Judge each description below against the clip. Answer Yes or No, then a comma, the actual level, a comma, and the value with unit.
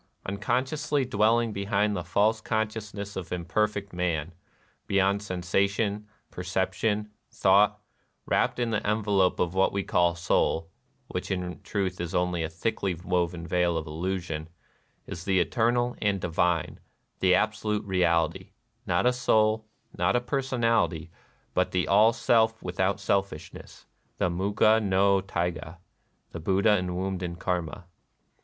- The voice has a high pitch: No, very low, 95 Hz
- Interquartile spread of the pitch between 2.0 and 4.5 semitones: Yes, average, 3.3 semitones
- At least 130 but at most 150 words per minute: Yes, average, 140 wpm